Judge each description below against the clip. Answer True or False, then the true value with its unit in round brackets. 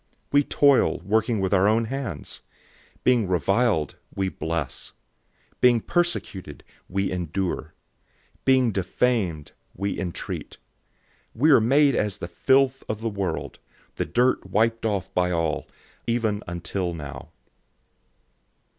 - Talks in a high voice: False (105 Hz)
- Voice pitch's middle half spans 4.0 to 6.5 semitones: True (5.2 semitones)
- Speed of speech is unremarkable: False (130 wpm)